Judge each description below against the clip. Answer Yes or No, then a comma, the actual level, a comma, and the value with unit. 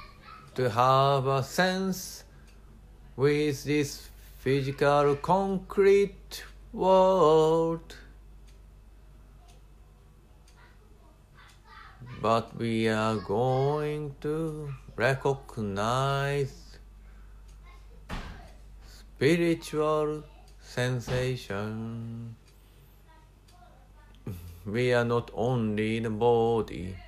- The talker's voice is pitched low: Yes, low, 130 Hz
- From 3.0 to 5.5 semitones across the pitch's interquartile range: Yes, average, 5.1 semitones